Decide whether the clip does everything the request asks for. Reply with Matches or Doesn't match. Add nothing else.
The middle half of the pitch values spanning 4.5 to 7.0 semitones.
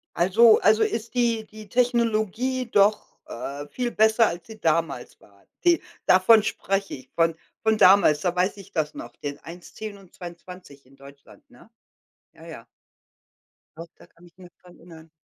Matches